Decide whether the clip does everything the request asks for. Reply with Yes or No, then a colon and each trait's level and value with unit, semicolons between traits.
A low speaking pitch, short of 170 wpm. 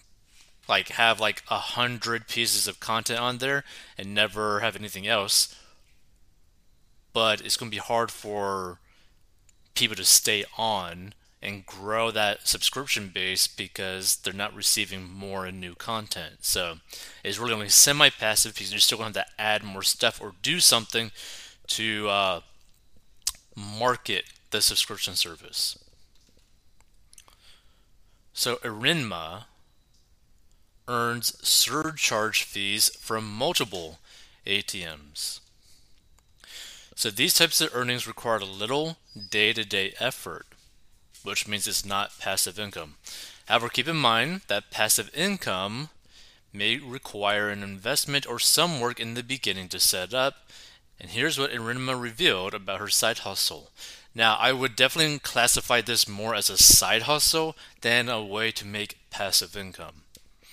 Yes: low, 105 Hz; slow, 135 wpm